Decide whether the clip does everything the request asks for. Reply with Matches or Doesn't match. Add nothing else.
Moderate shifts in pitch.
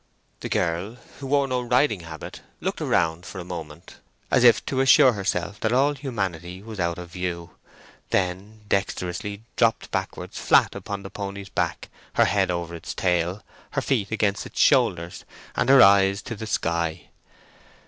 Matches